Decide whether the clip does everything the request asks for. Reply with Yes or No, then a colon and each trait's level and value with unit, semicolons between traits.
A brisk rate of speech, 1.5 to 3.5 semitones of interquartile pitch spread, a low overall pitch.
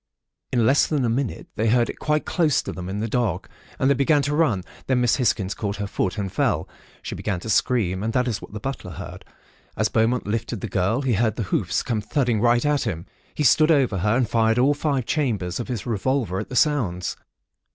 No: fast, 230 wpm; average, 4.5 semitones; low, 115 Hz